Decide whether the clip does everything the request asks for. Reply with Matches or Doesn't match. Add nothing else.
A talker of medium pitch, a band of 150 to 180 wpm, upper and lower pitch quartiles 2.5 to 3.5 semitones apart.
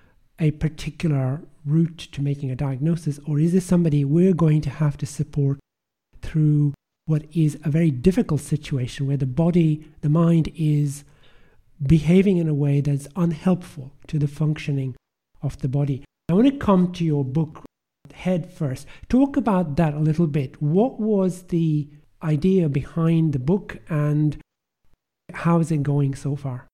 Matches